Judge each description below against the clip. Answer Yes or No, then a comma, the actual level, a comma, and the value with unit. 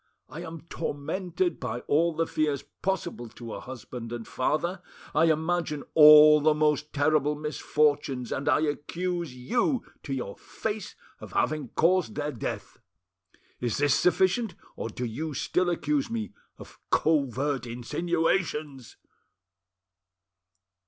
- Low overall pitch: No, medium, 150 Hz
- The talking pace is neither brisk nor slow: No, slow, 125 wpm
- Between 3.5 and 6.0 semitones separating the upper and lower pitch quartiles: Yes, average, 4.2 semitones